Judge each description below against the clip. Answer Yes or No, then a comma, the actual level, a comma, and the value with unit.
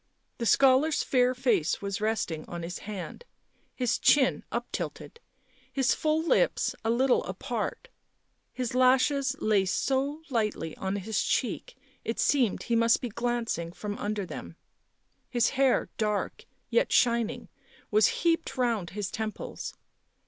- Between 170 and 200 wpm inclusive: No, average, 140 wpm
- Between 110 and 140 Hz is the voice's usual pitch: No, high, 235 Hz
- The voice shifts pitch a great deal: No, average, 4.1 semitones